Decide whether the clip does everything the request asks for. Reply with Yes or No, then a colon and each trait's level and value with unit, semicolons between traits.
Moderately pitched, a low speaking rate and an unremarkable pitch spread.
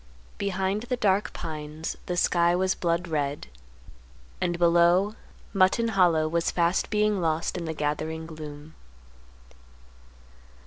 Yes: medium, 170 Hz; slow, 120 wpm; average, 3.0 semitones